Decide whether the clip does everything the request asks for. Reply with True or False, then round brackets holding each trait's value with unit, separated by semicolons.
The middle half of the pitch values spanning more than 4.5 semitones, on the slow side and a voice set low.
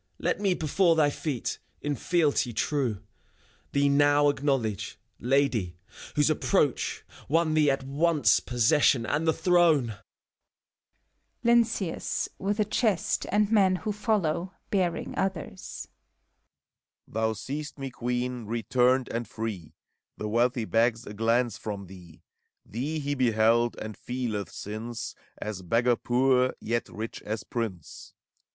True (5.6 semitones; 125 wpm; 130 Hz)